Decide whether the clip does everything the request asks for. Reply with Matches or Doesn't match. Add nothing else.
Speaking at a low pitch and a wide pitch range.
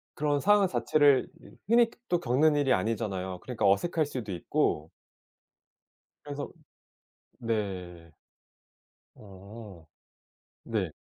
Matches